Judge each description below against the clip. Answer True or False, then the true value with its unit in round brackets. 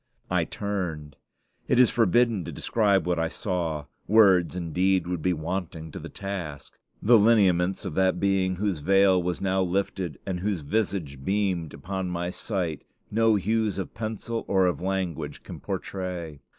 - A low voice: True (95 Hz)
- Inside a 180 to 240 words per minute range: False (160 wpm)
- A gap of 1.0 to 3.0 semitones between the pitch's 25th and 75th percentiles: True (2.6 semitones)